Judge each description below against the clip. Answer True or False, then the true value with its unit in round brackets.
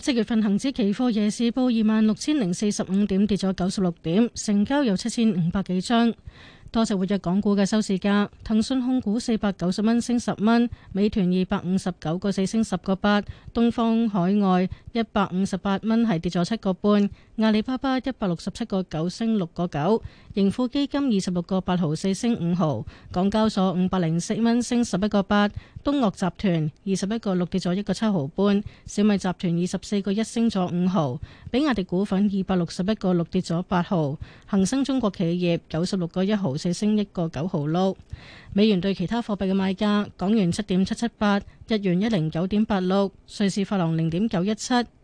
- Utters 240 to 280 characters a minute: False (300 characters per minute)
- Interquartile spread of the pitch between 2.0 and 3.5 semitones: True (3.2 semitones)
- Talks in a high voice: True (200 Hz)